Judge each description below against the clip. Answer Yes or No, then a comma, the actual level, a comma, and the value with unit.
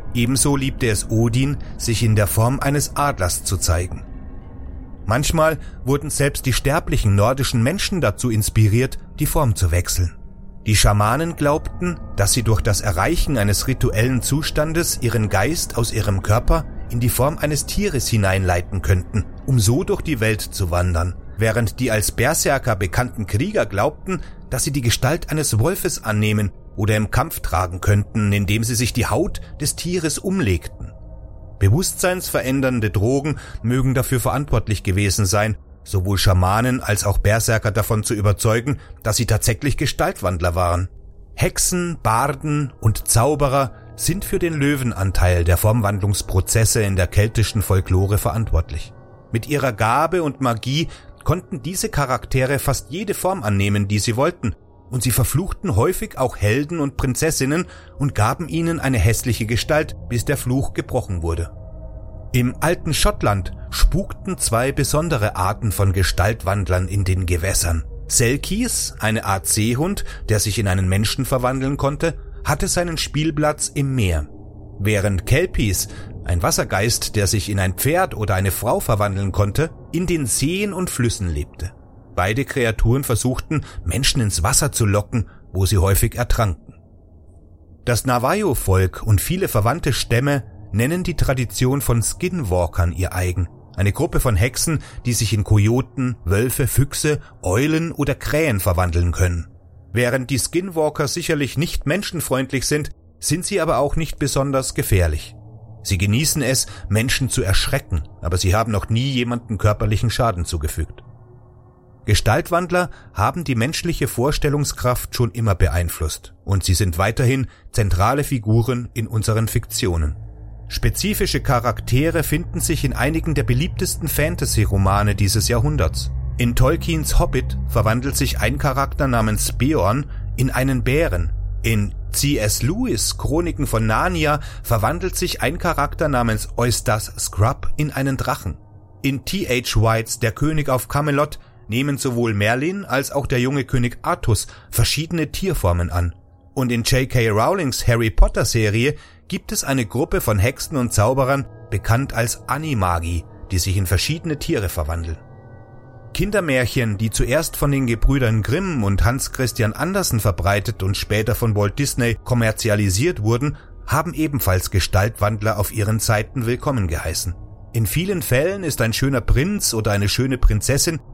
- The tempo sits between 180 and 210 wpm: No, average, 140 wpm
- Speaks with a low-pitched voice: Yes, low, 115 Hz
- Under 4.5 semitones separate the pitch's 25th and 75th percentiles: No, average, 5.3 semitones